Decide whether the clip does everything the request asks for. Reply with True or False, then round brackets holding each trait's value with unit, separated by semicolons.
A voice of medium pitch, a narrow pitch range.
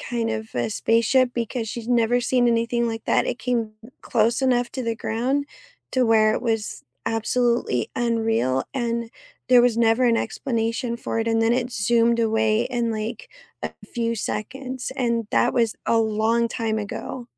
False (230 Hz; 1.5 semitones)